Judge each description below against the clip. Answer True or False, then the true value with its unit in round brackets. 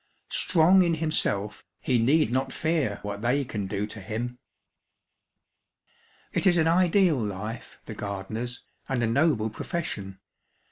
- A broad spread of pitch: True (7.2 semitones)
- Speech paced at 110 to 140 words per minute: True (135 wpm)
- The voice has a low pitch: True (125 Hz)